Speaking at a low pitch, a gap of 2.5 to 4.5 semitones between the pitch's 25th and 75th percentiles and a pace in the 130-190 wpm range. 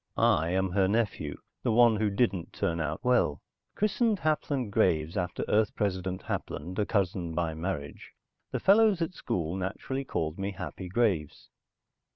No: very low, 95 Hz; wide, 5.5 semitones; average, 155 wpm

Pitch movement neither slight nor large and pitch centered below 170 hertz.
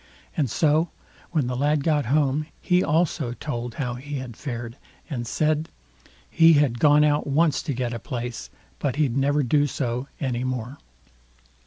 Yes: average, 3.6 semitones; medium, 140 Hz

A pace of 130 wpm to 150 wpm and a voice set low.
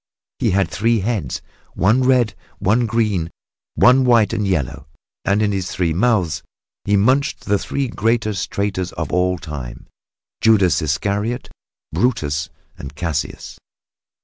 Yes: slow, 135 wpm; low, 100 Hz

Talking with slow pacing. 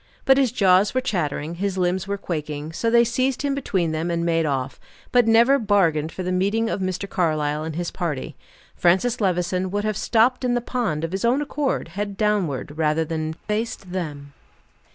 No: average, 195 wpm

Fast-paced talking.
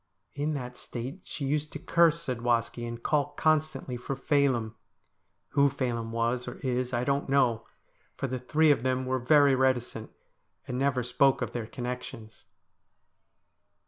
No: average, 150 wpm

